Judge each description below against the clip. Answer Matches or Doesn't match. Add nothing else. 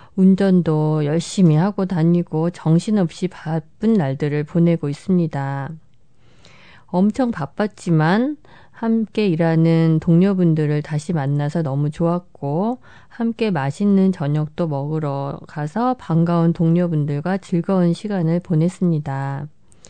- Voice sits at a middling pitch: Matches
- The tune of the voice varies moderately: Matches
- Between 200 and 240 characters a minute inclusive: Doesn't match